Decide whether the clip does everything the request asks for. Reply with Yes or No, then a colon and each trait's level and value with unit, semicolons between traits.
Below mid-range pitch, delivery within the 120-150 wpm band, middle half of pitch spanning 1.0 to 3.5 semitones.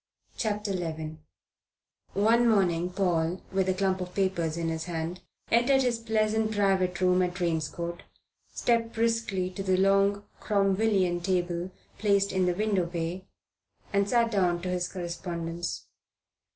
No: medium, 185 Hz; average, 140 wpm; average, 2.8 semitones